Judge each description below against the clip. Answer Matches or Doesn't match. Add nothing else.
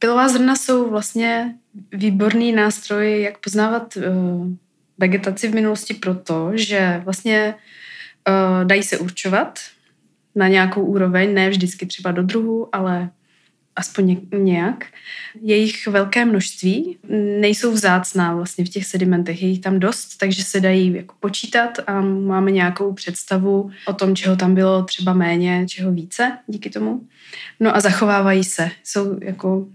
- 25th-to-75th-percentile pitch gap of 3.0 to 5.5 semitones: Doesn't match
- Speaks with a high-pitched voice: Matches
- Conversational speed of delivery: Matches